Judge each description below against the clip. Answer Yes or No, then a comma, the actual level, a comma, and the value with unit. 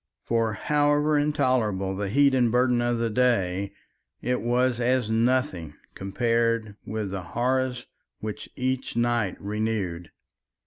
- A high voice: No, low, 120 Hz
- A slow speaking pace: Yes, slow, 125 wpm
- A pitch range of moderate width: Yes, average, 3.5 semitones